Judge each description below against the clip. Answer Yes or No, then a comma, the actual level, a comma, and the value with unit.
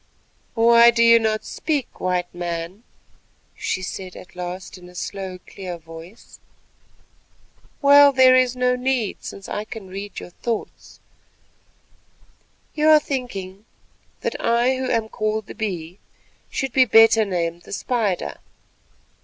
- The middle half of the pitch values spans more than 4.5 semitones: Yes, average, 5.2 semitones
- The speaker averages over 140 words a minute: No, slow, 135 wpm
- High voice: Yes, high, 215 Hz